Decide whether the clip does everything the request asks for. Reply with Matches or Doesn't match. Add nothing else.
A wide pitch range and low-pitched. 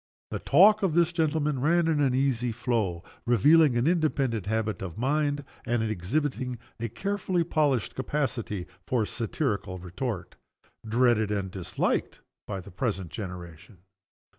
Matches